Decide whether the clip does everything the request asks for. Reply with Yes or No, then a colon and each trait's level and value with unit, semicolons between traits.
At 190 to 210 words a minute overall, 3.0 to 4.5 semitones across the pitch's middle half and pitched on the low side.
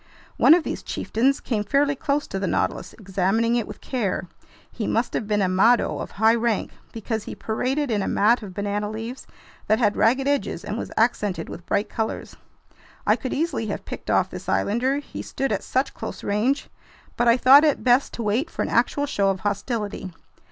No: average, 200 wpm; average, 4.1 semitones; high, 225 Hz